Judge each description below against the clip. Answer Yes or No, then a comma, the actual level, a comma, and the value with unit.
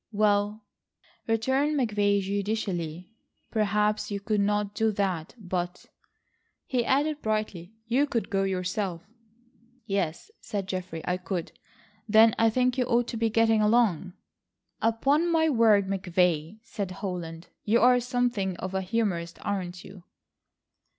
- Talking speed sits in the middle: No, slow, 130 wpm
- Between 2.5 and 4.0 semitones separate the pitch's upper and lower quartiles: Yes, average, 3.6 semitones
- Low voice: No, high, 205 Hz